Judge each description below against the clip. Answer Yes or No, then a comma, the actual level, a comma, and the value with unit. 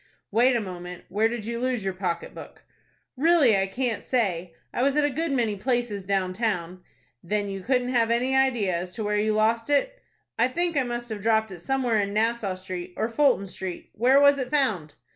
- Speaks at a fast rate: Yes, fast, 210 wpm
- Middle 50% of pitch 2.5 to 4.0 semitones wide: No, average, 4.8 semitones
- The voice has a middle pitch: No, high, 225 Hz